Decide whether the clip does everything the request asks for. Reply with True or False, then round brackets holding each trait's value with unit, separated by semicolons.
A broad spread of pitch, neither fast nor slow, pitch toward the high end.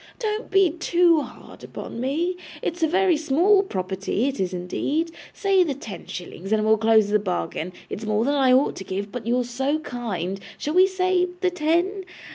True (8.8 semitones; 190 wpm; 275 Hz)